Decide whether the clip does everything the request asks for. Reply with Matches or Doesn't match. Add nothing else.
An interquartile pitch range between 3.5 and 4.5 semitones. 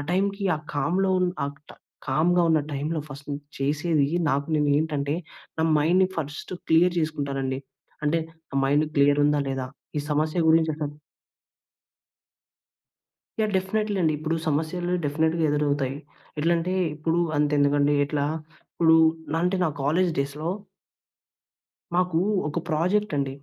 Doesn't match